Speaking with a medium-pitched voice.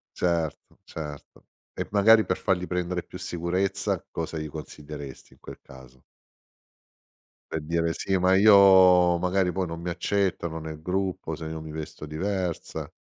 No: very low, 85 Hz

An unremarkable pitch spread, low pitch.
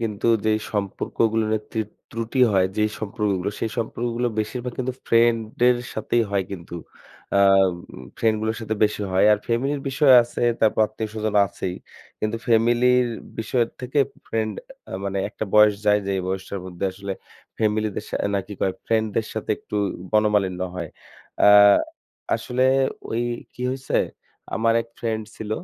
No: narrow, 2.2 semitones; low, 110 Hz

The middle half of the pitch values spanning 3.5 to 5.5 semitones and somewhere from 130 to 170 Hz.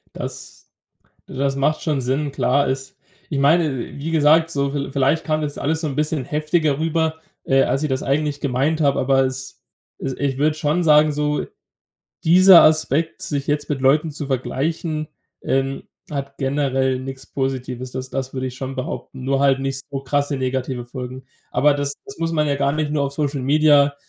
No: narrow, 2.4 semitones; medium, 140 Hz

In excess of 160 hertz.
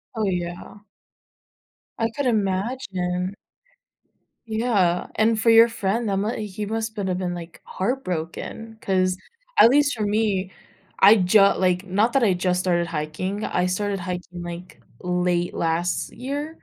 Yes: high, 190 Hz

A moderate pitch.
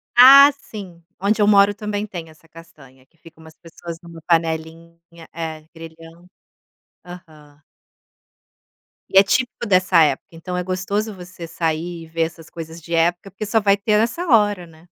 Yes: medium, 170 Hz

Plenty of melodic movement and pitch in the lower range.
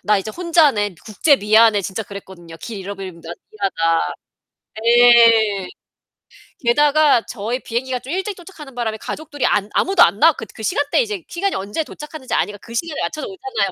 No: wide, 6.7 semitones; high, 235 Hz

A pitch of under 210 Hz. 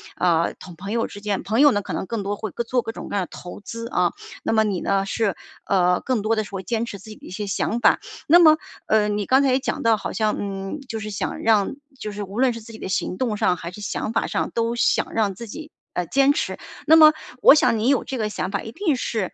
No: high, 215 Hz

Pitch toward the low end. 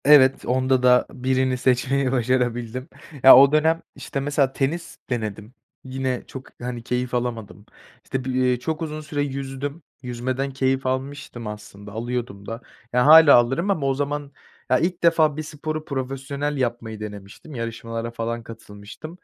Yes: low, 130 Hz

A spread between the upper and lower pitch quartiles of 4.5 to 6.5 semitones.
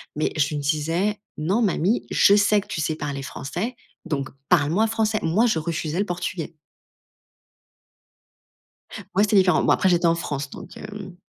Yes: average, 4.9 semitones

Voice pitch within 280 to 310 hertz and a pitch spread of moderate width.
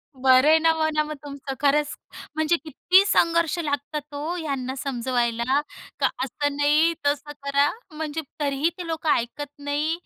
No: very high, 290 Hz; narrow, 2.2 semitones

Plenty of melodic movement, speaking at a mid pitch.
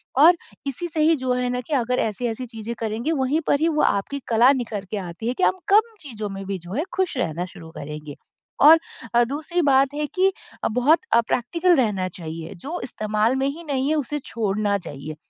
No: wide, 6.4 semitones; very high, 250 Hz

